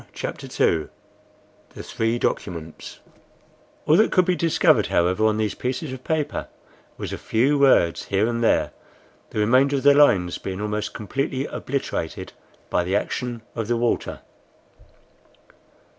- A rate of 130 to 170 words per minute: Yes, average, 145 wpm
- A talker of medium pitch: No, low, 115 Hz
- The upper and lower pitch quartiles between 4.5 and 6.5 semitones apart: Yes, average, 5.1 semitones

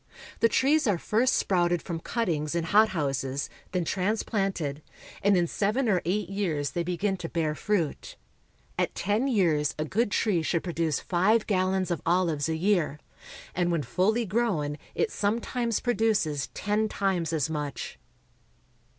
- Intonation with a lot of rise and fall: No, average, 4.6 semitones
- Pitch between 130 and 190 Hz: Yes, medium, 185 Hz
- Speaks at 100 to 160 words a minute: Yes, average, 150 wpm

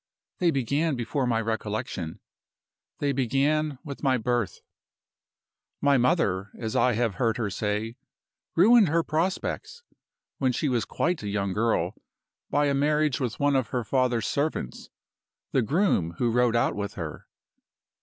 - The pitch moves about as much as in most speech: Yes, average, 4.7 semitones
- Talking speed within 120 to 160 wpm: Yes, average, 145 wpm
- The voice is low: Yes, low, 125 Hz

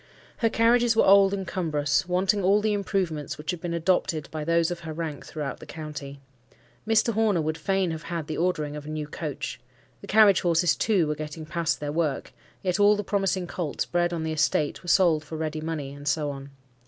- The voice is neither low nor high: Yes, medium, 165 Hz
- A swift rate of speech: Yes, fast, 215 wpm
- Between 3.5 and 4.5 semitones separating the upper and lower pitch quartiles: Yes, average, 4.0 semitones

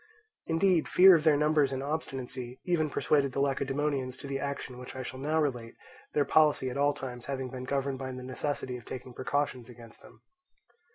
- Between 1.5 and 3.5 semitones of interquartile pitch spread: Yes, narrow, 2.5 semitones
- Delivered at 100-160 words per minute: No, average, 190 wpm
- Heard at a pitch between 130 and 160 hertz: Yes, low, 135 Hz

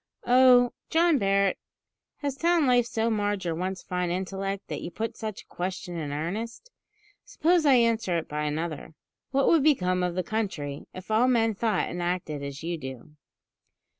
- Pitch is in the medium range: No, high, 195 Hz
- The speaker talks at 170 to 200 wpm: Yes, average, 175 wpm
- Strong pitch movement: Yes, wide, 5.8 semitones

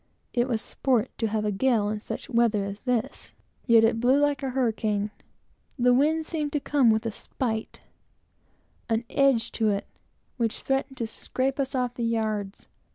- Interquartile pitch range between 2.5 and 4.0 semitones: Yes, average, 3.3 semitones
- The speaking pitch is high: Yes, high, 235 Hz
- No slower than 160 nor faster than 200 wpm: Yes, average, 175 wpm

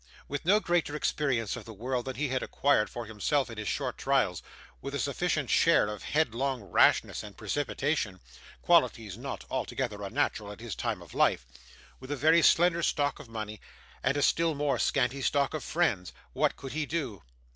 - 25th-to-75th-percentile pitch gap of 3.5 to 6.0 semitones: Yes, average, 4.8 semitones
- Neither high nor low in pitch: No, low, 130 Hz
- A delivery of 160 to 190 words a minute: Yes, average, 185 wpm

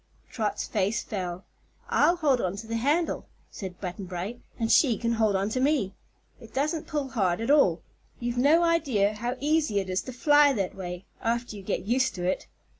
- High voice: Yes, high, 230 Hz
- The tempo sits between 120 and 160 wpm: No, average, 195 wpm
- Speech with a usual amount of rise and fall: No, wide, 6.1 semitones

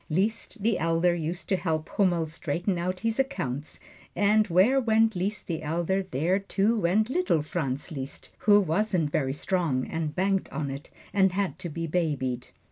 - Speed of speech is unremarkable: Yes, average, 170 wpm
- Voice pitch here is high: No, medium, 175 Hz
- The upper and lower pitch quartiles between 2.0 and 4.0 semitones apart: No, average, 4.5 semitones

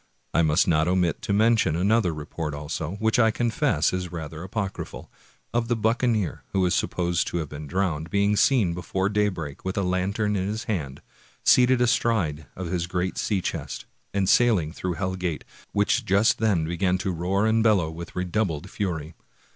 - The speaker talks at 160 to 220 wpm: Yes, average, 180 wpm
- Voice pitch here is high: No, very low, 95 Hz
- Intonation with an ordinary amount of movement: Yes, average, 4.1 semitones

